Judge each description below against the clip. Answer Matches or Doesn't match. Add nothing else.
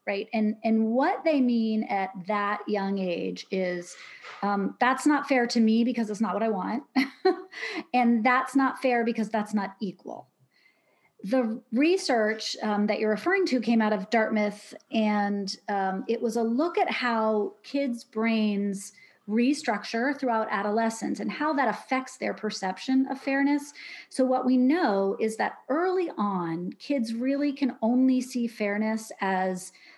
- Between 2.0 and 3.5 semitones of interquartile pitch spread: Doesn't match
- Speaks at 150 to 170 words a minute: Matches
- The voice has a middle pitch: Doesn't match